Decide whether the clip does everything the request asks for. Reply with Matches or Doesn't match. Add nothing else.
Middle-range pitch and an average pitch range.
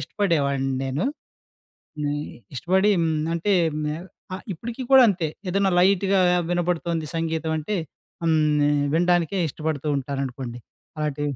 Matches